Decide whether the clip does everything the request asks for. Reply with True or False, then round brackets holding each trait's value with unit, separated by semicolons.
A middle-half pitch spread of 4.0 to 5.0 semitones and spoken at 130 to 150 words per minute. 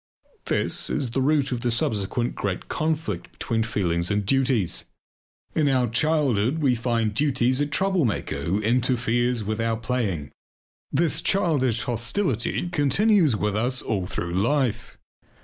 True (4.7 semitones; 135 wpm)